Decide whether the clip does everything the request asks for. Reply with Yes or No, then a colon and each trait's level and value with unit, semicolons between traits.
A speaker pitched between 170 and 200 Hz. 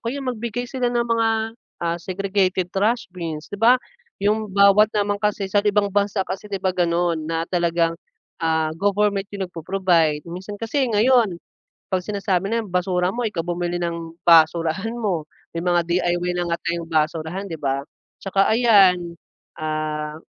Yes: medium, 185 Hz